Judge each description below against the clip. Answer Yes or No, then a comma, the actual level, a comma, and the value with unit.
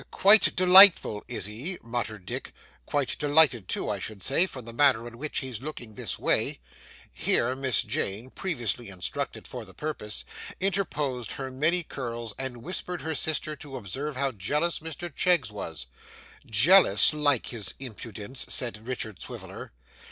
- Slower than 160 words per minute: Yes, average, 150 wpm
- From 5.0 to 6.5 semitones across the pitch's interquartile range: Yes, wide, 5.5 semitones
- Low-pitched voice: Yes, low, 130 Hz